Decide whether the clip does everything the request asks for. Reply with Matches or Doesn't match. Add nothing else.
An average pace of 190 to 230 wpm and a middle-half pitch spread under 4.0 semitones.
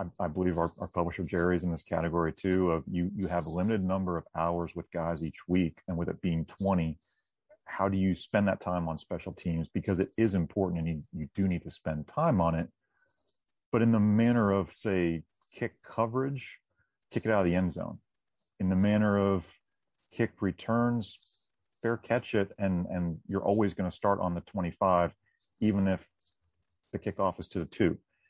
Matches